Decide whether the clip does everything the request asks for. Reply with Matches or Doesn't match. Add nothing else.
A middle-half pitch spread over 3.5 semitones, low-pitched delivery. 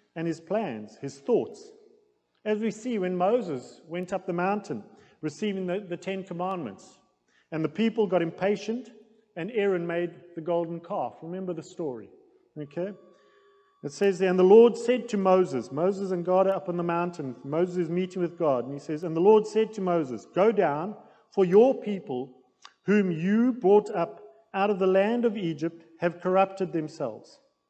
Doesn't match